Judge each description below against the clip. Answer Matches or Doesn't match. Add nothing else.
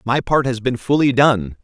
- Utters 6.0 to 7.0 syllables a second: Doesn't match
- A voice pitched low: Matches